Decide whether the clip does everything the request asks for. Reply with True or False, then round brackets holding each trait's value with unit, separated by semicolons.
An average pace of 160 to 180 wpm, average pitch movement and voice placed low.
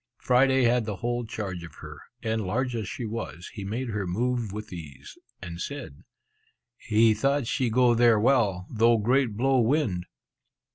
True (165 wpm; 3.5 semitones; 115 Hz)